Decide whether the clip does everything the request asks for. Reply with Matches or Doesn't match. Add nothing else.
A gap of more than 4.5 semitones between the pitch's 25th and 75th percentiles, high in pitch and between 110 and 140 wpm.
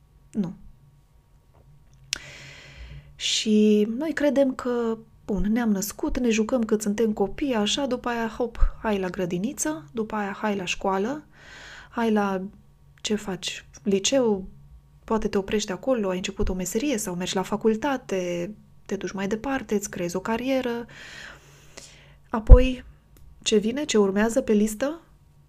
Doesn't match